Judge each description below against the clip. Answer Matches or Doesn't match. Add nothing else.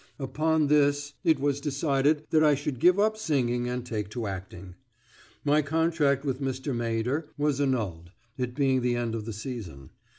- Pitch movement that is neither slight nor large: Matches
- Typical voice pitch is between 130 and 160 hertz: Matches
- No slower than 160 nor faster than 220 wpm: Matches